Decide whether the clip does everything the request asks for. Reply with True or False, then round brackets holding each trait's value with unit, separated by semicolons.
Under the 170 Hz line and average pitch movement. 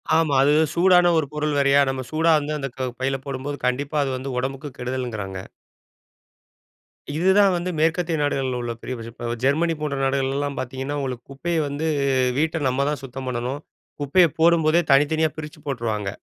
True (140 Hz; 3.4 semitones)